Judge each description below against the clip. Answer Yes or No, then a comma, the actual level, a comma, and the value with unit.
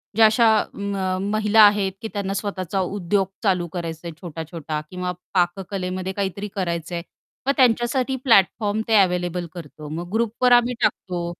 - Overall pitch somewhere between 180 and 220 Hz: Yes, high, 190 Hz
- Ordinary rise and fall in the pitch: Yes, average, 3.2 semitones